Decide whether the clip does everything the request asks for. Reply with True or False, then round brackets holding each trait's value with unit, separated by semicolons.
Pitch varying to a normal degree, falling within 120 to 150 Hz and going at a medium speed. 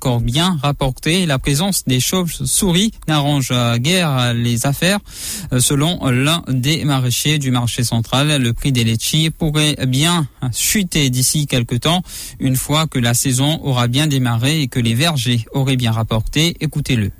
True (3.8 semitones; 135 Hz; 155 wpm)